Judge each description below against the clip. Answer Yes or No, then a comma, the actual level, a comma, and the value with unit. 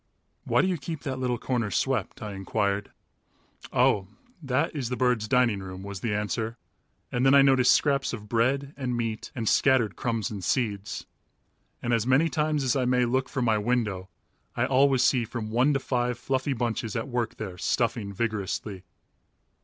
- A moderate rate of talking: Yes, average, 180 wpm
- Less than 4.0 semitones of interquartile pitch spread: Yes, average, 3.5 semitones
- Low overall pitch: Yes, low, 120 Hz